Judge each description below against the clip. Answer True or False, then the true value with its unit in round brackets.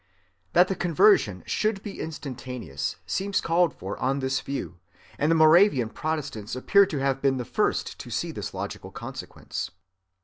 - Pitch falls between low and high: True (145 Hz)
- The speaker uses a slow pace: False (160 wpm)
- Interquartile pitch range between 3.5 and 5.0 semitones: False (5.6 semitones)